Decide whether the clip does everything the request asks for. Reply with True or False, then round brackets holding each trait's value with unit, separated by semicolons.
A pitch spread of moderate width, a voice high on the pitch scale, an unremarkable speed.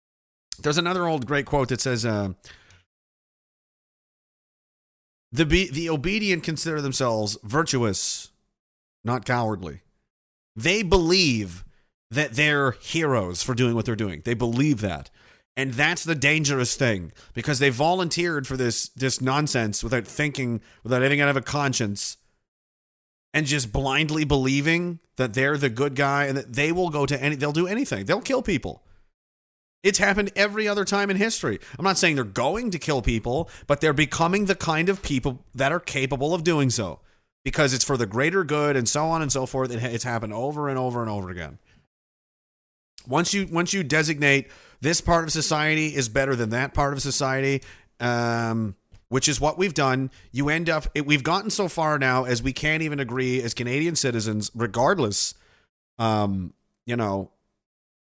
False (4.9 semitones; 135 Hz; 170 wpm)